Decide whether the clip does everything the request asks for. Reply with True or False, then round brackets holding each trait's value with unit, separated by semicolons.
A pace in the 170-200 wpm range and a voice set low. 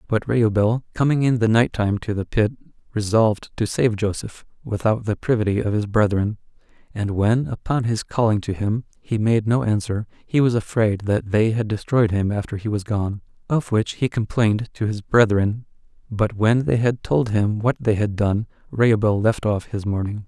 True (190 wpm; 110 Hz)